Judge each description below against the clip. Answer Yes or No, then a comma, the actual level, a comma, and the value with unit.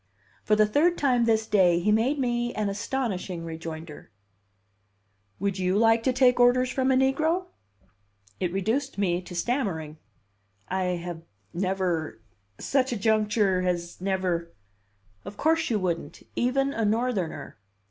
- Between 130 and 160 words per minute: Yes, average, 140 wpm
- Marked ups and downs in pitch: Yes, wide, 5.8 semitones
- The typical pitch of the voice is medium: No, high, 210 Hz